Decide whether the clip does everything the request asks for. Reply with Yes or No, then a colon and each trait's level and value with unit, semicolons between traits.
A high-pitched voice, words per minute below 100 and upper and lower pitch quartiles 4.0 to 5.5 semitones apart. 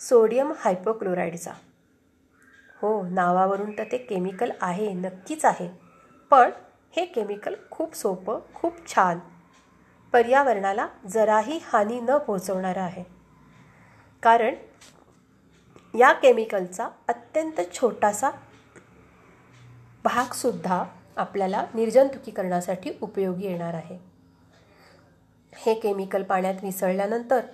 Yes: high, 200 Hz; average, 85 wpm; average, 4.6 semitones